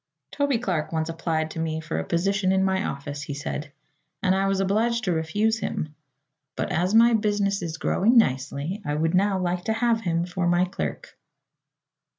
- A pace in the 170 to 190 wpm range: Yes, average, 185 wpm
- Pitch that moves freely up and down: No, average, 4.3 semitones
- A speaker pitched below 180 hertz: No, medium, 185 Hz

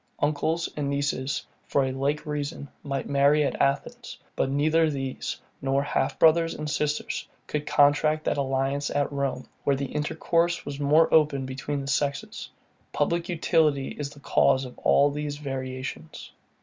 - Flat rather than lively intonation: Yes, narrow, 1.7 semitones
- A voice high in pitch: No, medium, 145 Hz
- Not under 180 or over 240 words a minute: No, average, 155 wpm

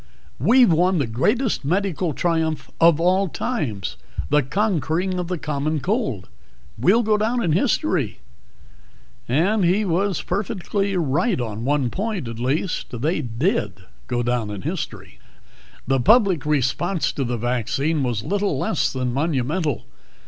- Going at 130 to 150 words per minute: Yes, average, 140 wpm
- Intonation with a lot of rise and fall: Yes, wide, 7.2 semitones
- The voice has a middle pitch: Yes, medium, 160 Hz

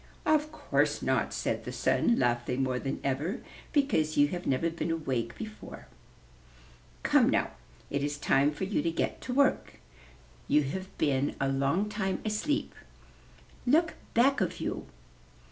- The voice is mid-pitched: Yes, medium, 165 Hz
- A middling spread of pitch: No, wide, 7.9 semitones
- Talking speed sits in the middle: Yes, average, 150 wpm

